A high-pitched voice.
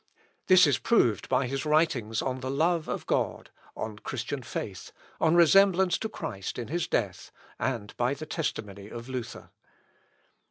No: low, 130 Hz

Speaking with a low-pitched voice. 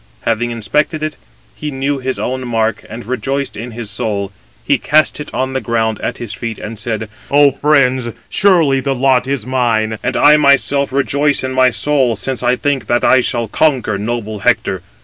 Yes: low, 130 Hz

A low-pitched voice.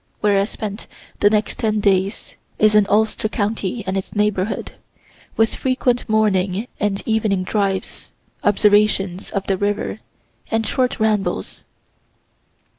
No: high, 210 Hz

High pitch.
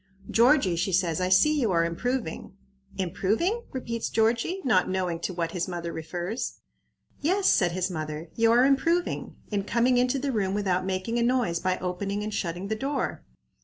Yes: high, 200 Hz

